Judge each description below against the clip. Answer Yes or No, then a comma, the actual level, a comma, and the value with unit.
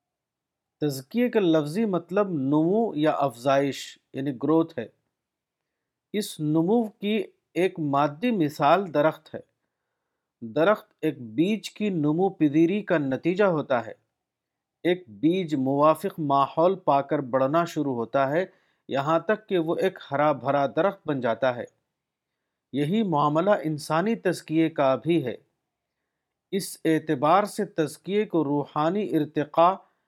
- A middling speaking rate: Yes, average, 125 wpm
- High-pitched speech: No, medium, 160 Hz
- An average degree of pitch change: Yes, average, 4.6 semitones